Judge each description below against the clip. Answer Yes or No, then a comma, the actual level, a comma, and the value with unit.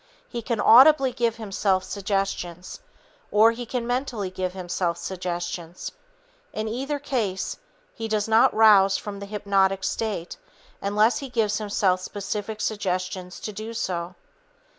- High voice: Yes, high, 205 Hz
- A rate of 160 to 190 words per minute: No, slow, 135 wpm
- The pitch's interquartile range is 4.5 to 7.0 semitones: No, average, 3.2 semitones